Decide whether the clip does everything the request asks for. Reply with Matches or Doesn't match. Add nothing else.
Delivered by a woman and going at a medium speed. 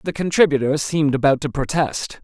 Doesn't match